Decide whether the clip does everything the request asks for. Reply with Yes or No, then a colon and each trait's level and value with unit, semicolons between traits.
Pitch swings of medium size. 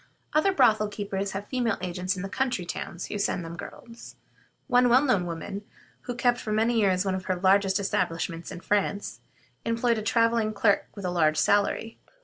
Yes: average, 3.9 semitones